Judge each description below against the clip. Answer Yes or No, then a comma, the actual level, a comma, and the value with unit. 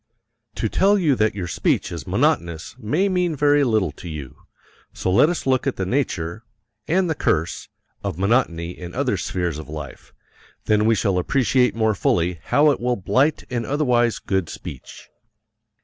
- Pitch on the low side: Yes, low, 110 Hz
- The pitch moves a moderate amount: No, wide, 7.9 semitones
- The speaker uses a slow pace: No, average, 170 wpm